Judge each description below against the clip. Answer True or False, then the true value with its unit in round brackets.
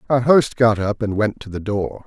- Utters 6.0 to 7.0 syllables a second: False (4.8 syllables/s)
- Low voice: True (110 Hz)